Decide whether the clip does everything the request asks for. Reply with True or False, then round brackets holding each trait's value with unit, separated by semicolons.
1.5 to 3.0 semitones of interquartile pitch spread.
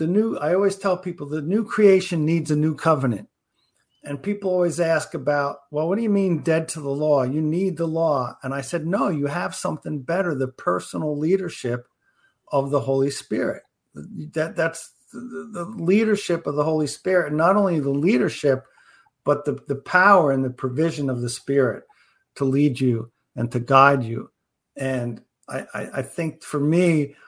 False (4.1 semitones)